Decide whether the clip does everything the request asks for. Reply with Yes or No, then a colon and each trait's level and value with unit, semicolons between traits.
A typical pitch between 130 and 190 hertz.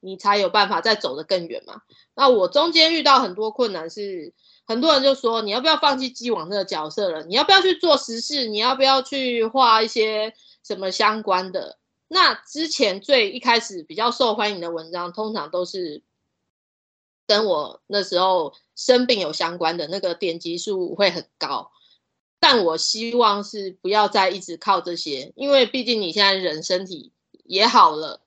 No: high, 215 Hz